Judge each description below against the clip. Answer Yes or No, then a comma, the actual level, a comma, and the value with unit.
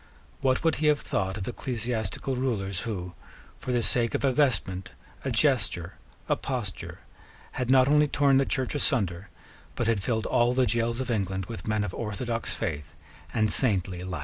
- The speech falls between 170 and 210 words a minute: Yes, average, 175 wpm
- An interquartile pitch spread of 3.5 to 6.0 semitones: Yes, average, 5.0 semitones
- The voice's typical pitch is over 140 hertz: No, low, 115 Hz